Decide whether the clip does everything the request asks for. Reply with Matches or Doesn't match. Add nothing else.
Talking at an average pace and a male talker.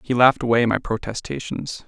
Matches